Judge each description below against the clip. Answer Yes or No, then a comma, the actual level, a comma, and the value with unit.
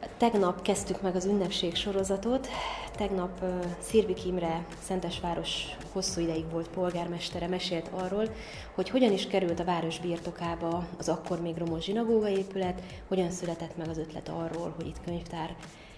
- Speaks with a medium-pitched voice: Yes, medium, 180 Hz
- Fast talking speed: No, average, 145 wpm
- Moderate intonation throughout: No, narrow, 2.2 semitones